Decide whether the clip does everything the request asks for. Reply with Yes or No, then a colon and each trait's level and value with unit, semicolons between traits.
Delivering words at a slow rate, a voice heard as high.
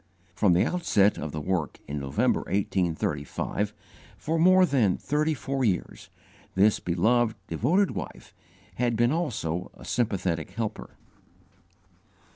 No: slow, 120 wpm; low, 105 Hz